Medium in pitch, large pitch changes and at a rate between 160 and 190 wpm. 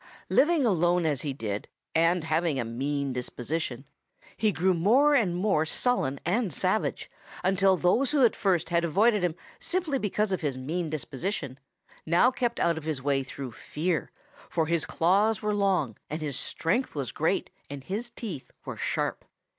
Yes: medium, 170 Hz; wide, 6.4 semitones; average, 170 wpm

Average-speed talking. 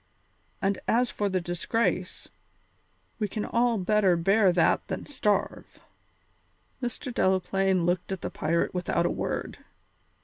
No: slow, 130 wpm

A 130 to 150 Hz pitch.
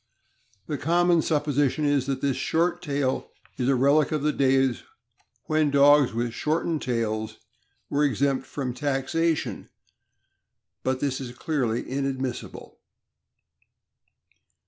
Yes: medium, 140 Hz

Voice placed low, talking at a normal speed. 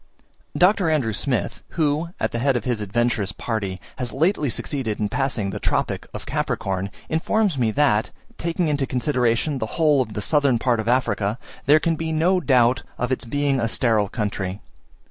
Yes: low, 125 Hz; average, 180 wpm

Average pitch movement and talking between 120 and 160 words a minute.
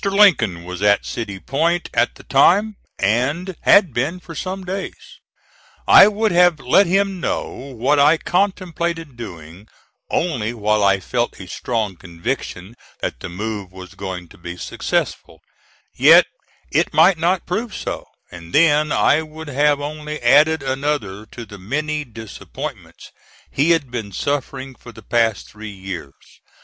No: wide, 8.1 semitones; average, 150 wpm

